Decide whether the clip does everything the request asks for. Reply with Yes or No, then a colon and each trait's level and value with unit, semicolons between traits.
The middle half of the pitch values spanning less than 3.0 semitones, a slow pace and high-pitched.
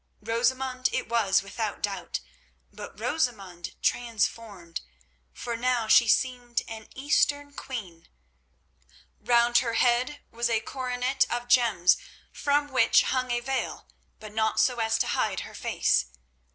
Yes: narrow, 2.6 semitones; slow, 130 wpm; high, 240 Hz